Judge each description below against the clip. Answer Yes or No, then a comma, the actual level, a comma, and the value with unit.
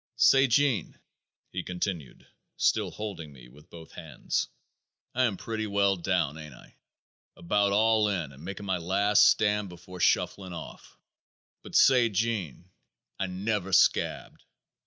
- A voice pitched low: Yes, very low, 95 Hz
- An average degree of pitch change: Yes, average, 3.6 semitones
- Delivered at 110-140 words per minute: Yes, slow, 135 wpm